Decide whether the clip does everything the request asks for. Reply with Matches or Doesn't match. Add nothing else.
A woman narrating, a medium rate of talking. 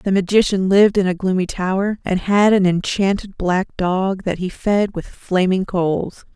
Matches